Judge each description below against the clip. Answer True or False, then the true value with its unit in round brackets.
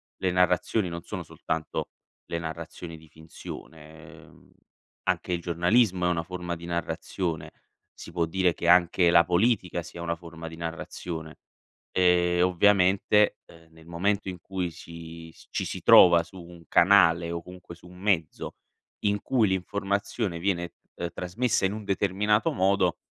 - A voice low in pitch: True (90 Hz)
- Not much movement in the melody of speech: True (2.1 semitones)